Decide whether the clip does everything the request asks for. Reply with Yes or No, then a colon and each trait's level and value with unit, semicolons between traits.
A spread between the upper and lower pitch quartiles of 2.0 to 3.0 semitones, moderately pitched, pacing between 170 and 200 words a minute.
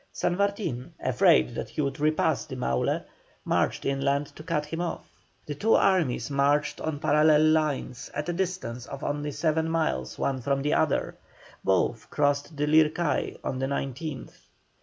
No: narrow, 2.6 semitones; medium, 145 Hz; average, 160 wpm